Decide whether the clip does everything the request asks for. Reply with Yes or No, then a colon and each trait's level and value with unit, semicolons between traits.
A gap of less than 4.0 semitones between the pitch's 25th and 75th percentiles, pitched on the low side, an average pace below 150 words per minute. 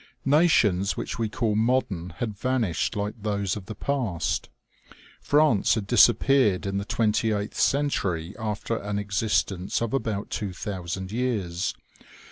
Yes: average, 3.4 semitones; low, 105 Hz; average, 140 wpm